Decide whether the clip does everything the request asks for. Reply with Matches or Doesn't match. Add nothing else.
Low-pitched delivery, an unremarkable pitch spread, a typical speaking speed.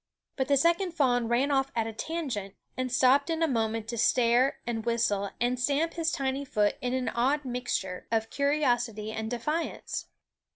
Doesn't match